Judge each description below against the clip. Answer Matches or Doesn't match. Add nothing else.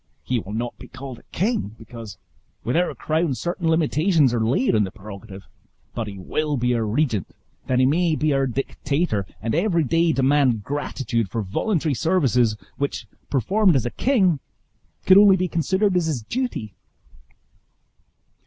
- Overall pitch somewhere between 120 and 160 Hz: Matches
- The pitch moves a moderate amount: Doesn't match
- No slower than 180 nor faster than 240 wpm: Doesn't match